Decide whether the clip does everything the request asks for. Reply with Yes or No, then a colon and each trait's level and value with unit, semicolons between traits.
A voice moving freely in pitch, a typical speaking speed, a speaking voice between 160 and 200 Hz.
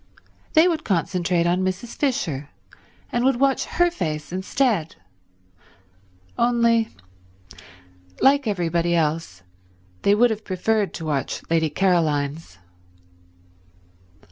No: wide, 6.5 semitones; slow, 100 wpm; medium, 185 Hz